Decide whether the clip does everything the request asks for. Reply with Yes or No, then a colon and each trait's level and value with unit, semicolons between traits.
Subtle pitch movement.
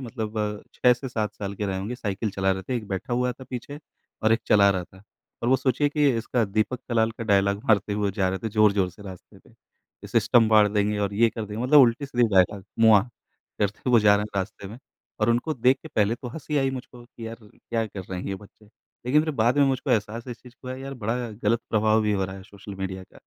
No: average, 3.5 semitones